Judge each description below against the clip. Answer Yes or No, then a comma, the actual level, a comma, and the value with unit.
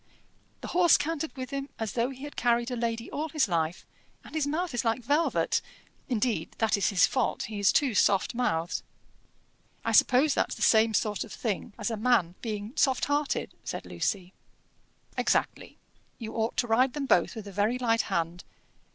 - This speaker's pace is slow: No, average, 185 wpm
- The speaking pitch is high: Yes, high, 235 Hz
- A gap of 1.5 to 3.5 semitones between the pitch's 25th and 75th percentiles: No, average, 4.4 semitones